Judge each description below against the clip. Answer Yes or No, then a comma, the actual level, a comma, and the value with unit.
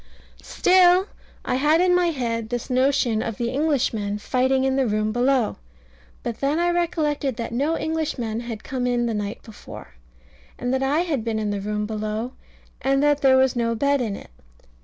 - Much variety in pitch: No, average, 4.2 semitones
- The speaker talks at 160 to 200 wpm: Yes, average, 185 wpm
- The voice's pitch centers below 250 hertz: No, very high, 255 Hz